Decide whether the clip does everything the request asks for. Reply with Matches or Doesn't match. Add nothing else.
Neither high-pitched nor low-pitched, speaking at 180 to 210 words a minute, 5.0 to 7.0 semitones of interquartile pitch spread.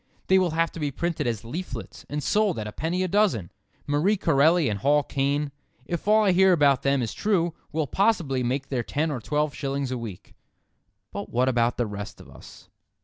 Matches